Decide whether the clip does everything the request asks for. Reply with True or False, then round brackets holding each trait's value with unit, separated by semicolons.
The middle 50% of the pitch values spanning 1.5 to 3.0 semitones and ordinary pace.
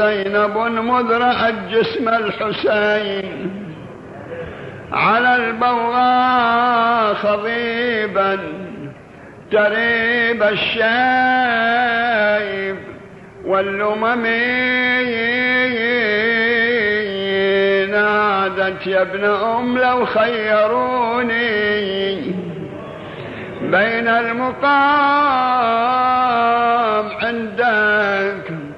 False (2.6 semitones; 40 wpm)